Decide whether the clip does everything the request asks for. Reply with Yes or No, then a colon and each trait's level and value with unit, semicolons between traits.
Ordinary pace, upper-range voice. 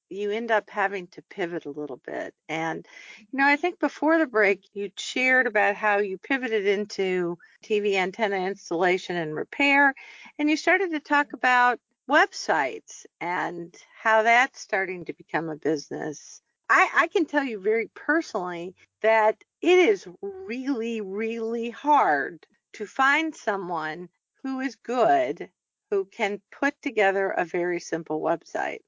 Yes: average, 150 wpm; high, 220 Hz